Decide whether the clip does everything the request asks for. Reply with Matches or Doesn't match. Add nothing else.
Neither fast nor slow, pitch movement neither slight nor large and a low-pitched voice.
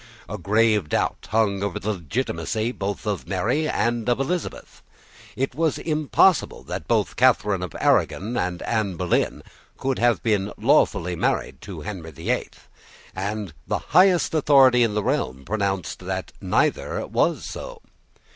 Matches